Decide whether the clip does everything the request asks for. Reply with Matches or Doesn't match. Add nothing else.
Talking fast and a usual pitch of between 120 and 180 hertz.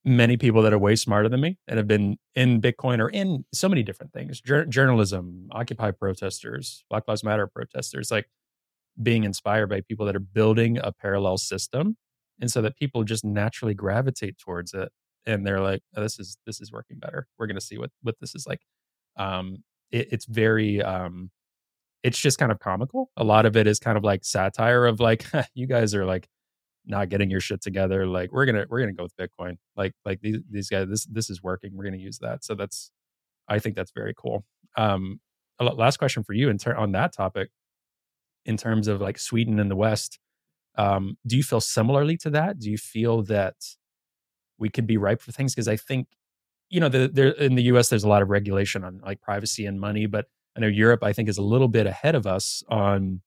Doesn't match